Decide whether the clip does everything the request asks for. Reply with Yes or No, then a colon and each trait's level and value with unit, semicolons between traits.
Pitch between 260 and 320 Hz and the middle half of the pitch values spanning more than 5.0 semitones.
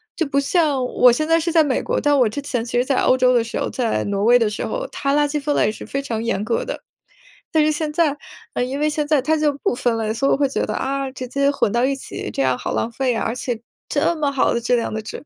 No: very high, 270 Hz; average, 3.8 semitones